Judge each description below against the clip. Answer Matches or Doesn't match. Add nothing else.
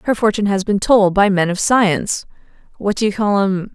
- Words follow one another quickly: Matches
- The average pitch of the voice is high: Matches